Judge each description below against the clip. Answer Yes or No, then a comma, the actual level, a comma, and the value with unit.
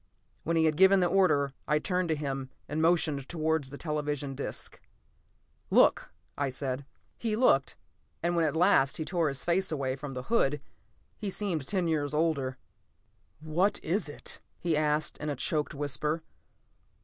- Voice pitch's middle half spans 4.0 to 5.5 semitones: No, average, 3.4 semitones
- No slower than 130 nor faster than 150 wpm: No, average, 165 wpm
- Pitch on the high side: No, medium, 155 Hz